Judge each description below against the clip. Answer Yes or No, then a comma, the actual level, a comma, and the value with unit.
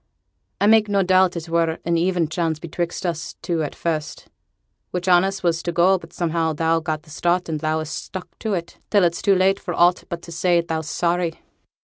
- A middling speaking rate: No, fast, 210 wpm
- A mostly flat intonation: Yes, narrow, 1.9 semitones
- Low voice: No, medium, 170 Hz